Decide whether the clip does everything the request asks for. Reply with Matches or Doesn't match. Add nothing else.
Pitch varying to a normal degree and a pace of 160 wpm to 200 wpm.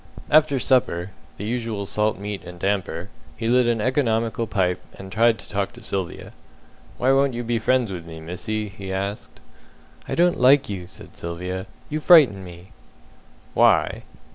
Matches